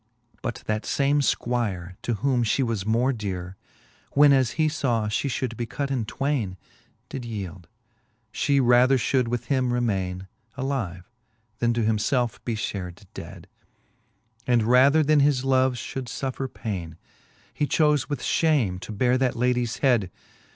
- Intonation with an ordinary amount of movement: Yes, average, 4.0 semitones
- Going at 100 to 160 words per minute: Yes, average, 155 wpm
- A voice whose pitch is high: No, low, 120 Hz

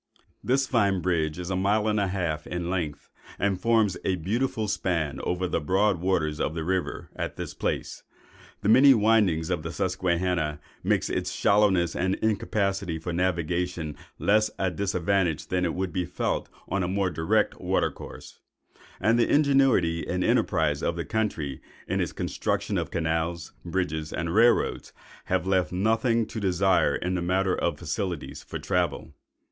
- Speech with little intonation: No, average, 3.2 semitones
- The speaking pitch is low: Yes, very low, 90 Hz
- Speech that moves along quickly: No, average, 165 wpm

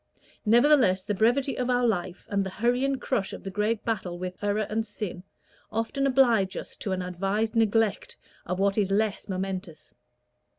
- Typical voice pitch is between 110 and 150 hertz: No, high, 210 Hz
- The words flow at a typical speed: Yes, average, 175 wpm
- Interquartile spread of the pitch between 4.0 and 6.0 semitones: No, average, 3.3 semitones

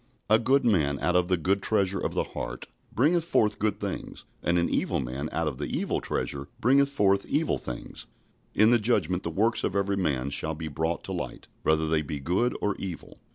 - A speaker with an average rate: No, fast, 210 wpm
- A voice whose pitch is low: Yes, very low, 90 Hz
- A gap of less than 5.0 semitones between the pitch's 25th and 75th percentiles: No, wide, 5.6 semitones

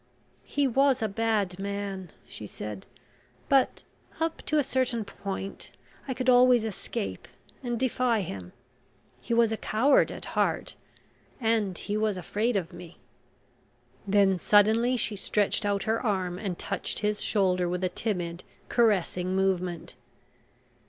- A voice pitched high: Yes, high, 205 Hz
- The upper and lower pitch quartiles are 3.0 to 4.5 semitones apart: Yes, average, 4.0 semitones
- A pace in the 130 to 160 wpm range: Yes, average, 140 wpm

